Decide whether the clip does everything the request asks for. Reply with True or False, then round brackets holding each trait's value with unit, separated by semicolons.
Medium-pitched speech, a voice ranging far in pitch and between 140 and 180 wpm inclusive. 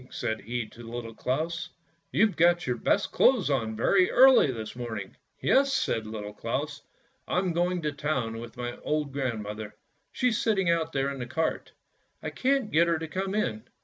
False (145 Hz; 7.2 semitones; 190 wpm)